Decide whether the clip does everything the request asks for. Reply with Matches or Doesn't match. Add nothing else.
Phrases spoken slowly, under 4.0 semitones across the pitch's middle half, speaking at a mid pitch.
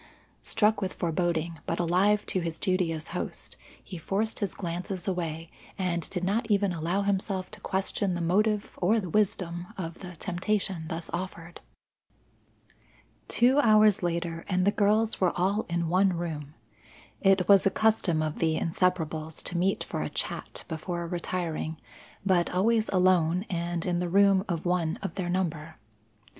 Doesn't match